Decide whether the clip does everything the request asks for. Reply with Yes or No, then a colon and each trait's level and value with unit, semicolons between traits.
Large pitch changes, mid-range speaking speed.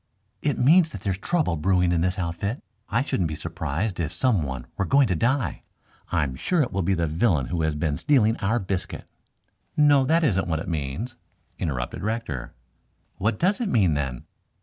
Yes: wide, 7.4 semitones; average, 190 wpm